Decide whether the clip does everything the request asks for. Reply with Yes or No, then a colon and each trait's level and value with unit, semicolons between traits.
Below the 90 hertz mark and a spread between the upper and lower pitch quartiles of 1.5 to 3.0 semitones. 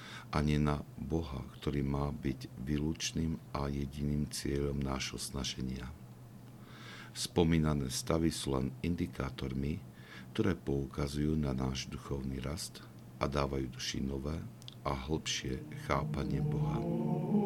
Yes: very low, 70 Hz; narrow, 2.4 semitones